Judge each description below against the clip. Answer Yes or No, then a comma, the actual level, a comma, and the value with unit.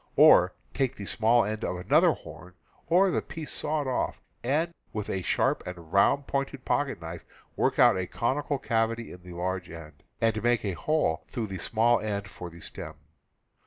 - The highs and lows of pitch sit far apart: Yes, wide, 6.7 semitones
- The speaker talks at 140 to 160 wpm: No, average, 185 wpm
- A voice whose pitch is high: No, low, 110 Hz